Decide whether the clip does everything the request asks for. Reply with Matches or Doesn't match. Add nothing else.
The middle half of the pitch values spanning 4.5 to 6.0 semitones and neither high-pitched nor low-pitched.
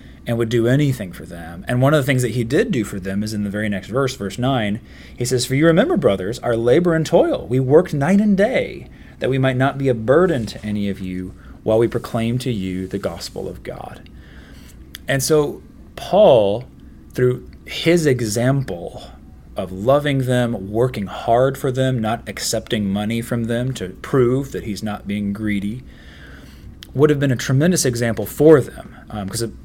Doesn't match